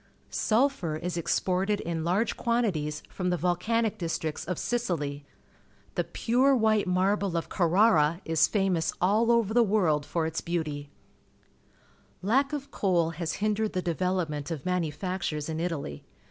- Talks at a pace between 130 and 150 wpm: Yes, average, 145 wpm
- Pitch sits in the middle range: Yes, medium, 180 Hz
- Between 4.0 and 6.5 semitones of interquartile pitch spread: Yes, average, 4.8 semitones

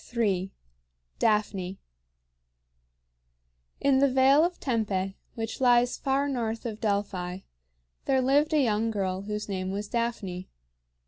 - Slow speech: Yes, slow, 120 wpm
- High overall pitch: Yes, high, 220 Hz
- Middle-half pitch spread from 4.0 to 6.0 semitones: Yes, average, 5.1 semitones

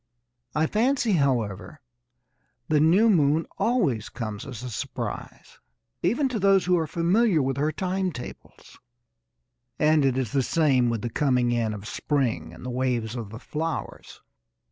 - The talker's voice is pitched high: No, medium, 145 Hz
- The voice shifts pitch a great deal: Yes, wide, 6.4 semitones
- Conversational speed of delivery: Yes, average, 155 wpm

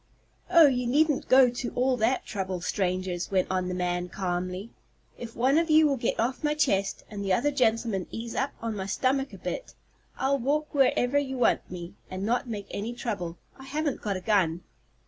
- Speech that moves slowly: No, average, 200 wpm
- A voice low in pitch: No, high, 230 Hz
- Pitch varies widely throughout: Yes, wide, 6.1 semitones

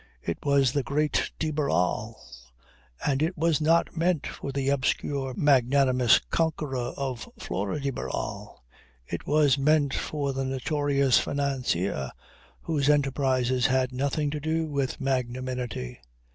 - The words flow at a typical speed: No, slow, 130 wpm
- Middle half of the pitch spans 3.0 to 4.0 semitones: No, narrow, 2.5 semitones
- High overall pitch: No, medium, 140 Hz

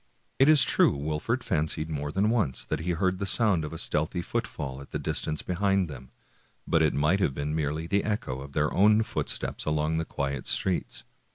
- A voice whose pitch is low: Yes, very low, 80 Hz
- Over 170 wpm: Yes, fast, 205 wpm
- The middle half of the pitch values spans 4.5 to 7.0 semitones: Yes, average, 4.8 semitones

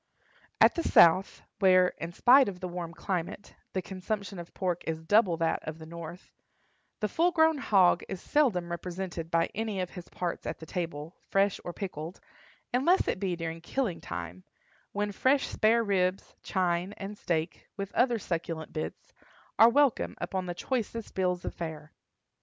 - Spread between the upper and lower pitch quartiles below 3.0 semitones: No, average, 3.6 semitones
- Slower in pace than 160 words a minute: No, average, 170 wpm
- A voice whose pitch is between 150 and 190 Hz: Yes, medium, 185 Hz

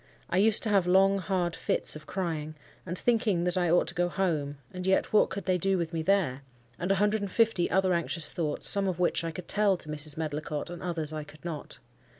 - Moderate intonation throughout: Yes, average, 3.6 semitones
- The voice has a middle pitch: Yes, medium, 175 Hz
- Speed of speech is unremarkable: No, fast, 225 wpm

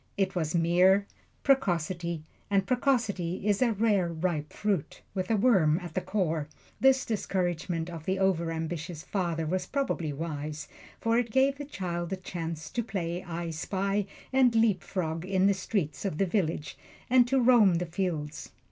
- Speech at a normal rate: Yes, average, 160 wpm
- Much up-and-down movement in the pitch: No, average, 3.9 semitones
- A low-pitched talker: No, medium, 185 Hz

